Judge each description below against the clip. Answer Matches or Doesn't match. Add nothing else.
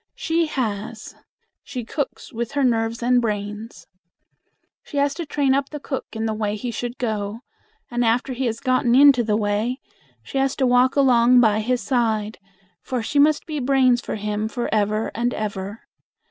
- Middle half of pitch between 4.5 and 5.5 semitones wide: Doesn't match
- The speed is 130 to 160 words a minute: Doesn't match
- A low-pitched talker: Doesn't match